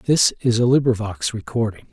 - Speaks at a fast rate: No, average, 155 wpm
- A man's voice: Yes, male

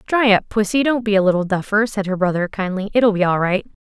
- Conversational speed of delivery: No, fast, 250 wpm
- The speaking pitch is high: Yes, high, 205 Hz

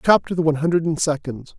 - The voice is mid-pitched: Yes, medium, 160 Hz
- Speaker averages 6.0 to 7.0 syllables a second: Yes, 6.9 syllables/s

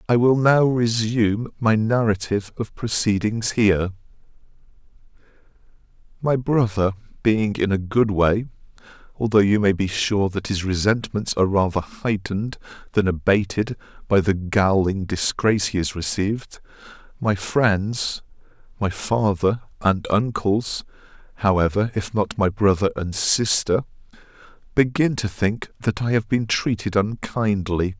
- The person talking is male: Yes, male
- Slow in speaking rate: Yes, slow, 120 wpm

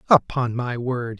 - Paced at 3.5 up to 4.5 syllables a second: Yes, 4.0 syllables/s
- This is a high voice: No, low, 125 Hz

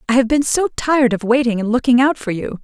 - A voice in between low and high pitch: No, very high, 250 Hz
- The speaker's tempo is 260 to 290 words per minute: Yes, fast, 275 wpm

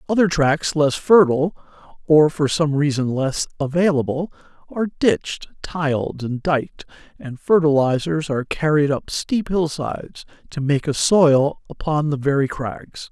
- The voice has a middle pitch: Yes, medium, 150 Hz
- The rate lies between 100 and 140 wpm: Yes, slow, 135 wpm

